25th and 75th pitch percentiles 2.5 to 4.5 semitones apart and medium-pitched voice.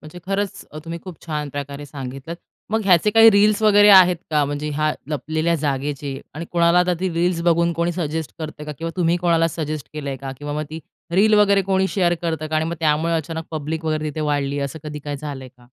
Yes: average, 2.9 semitones; medium, 160 Hz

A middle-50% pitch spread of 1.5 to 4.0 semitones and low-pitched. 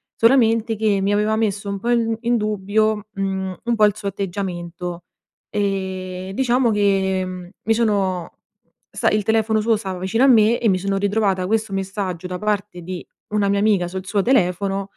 No: narrow, 2.5 semitones; high, 200 Hz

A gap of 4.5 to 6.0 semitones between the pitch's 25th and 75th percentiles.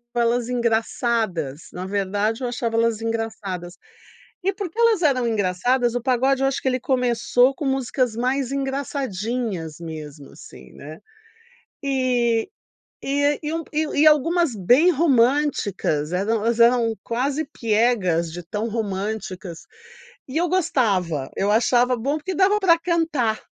Yes: average, 4.9 semitones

